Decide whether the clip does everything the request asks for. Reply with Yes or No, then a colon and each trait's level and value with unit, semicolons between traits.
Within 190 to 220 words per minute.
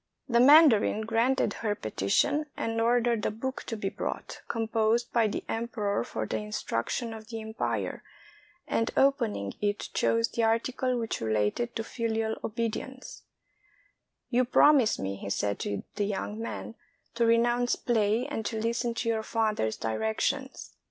No: average, 150 wpm